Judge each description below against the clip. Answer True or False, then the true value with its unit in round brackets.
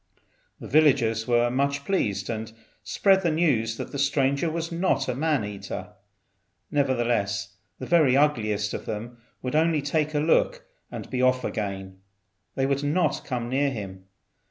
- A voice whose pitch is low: True (130 Hz)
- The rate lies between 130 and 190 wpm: True (155 wpm)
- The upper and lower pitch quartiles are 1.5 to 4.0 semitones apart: False (5.1 semitones)